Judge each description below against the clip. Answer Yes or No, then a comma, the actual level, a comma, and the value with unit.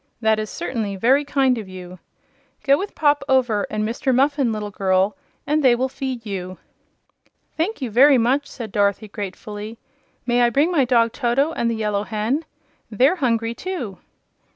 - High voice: Yes, high, 235 Hz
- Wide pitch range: No, average, 4.5 semitones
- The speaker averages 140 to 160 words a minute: No, average, 170 wpm